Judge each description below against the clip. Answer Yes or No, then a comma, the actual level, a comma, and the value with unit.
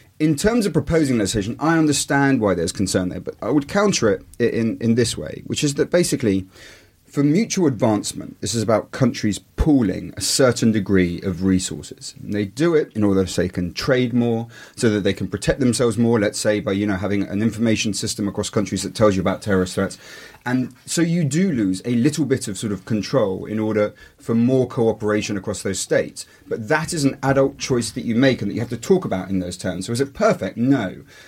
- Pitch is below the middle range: Yes, low, 115 Hz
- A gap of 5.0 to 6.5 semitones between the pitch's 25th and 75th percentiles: Yes, wide, 5.4 semitones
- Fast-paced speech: Yes, fast, 225 wpm